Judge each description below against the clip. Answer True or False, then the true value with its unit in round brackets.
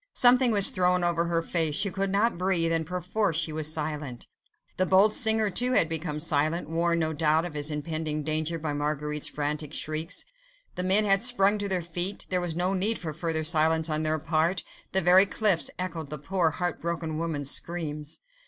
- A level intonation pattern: False (3.1 semitones)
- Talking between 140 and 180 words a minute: False (195 wpm)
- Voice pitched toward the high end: False (165 Hz)